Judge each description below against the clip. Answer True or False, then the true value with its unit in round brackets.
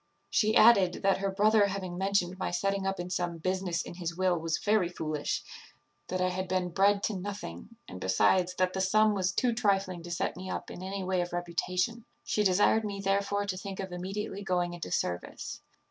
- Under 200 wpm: False (205 wpm)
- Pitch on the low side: False (185 Hz)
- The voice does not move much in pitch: True (2.1 semitones)